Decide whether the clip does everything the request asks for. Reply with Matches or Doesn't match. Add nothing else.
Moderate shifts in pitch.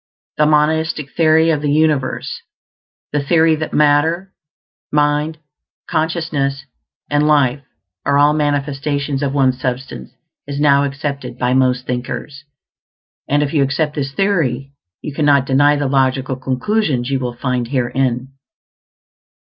Doesn't match